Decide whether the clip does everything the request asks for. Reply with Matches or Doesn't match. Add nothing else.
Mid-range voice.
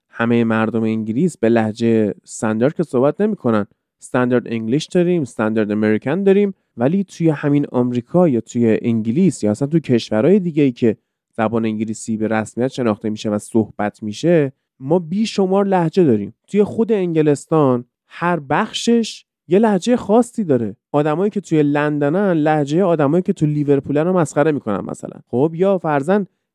Matches